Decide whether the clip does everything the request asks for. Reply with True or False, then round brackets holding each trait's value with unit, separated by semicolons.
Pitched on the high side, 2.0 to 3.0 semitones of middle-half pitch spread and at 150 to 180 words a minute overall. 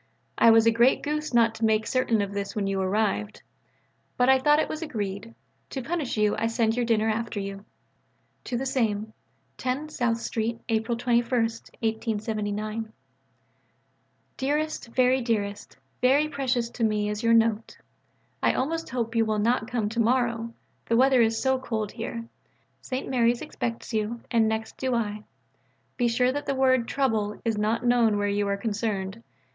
True (230 Hz; 2.6 semitones; 170 wpm)